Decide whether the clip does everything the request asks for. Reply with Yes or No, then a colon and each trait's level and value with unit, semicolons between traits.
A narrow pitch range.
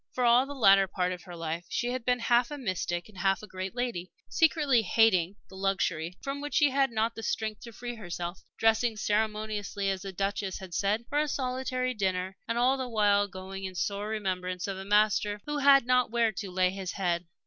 No: average, 4.4 semitones